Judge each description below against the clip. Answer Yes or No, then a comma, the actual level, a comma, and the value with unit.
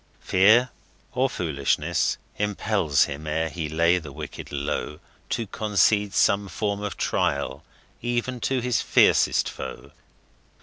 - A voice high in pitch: No, low, 100 Hz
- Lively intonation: Yes, wide, 5.9 semitones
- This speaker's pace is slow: Yes, slow, 125 wpm